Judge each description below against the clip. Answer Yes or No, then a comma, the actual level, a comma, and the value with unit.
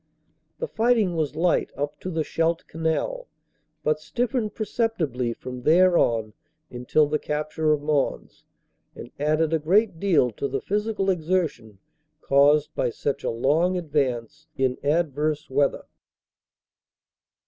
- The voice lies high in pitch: No, medium, 155 Hz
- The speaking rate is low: Yes, slow, 130 wpm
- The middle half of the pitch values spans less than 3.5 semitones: No, average, 4.2 semitones